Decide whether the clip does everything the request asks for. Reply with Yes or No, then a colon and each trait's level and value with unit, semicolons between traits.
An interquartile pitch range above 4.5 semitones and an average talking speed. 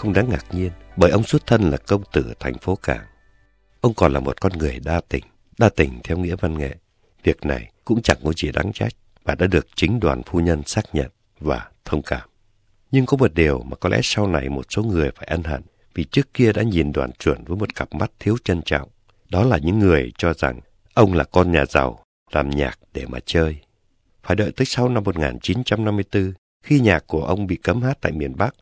Yes: average, 5.3 semitones; average, 230 wpm